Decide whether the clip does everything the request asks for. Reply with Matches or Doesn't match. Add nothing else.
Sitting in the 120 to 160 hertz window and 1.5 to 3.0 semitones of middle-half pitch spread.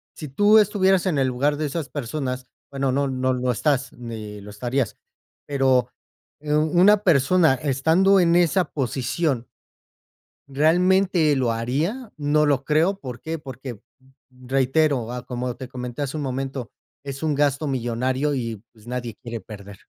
Doesn't match